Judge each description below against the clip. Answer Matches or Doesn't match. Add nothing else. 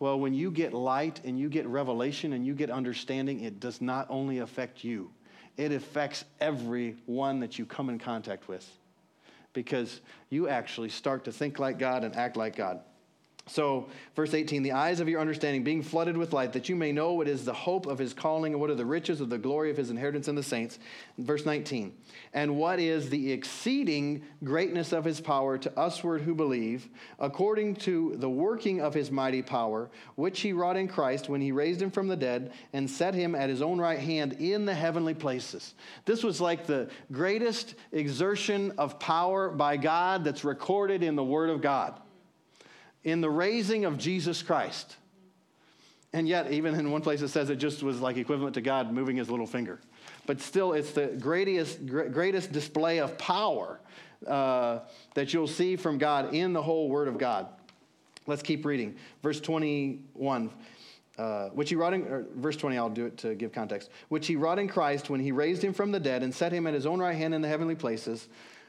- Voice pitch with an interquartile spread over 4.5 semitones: Doesn't match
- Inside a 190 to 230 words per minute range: Matches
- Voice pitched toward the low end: Doesn't match